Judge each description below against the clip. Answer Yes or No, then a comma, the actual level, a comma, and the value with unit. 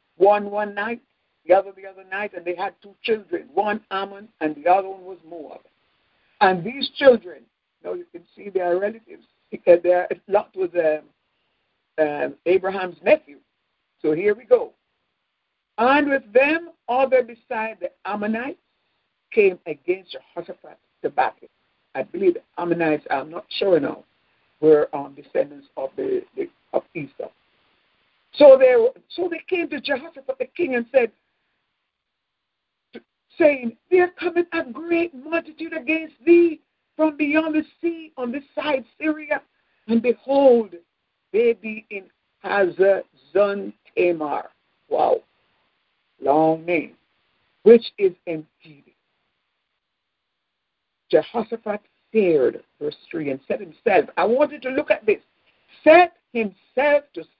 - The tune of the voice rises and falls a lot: Yes, wide, 9.0 semitones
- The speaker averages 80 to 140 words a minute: Yes, slow, 135 wpm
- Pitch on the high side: Yes, very high, 255 Hz